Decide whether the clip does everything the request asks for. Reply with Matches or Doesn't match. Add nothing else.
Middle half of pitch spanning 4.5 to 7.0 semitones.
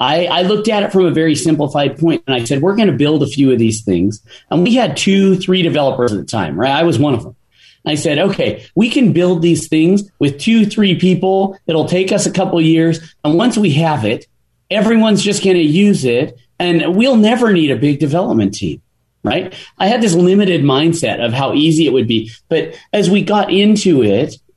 Matches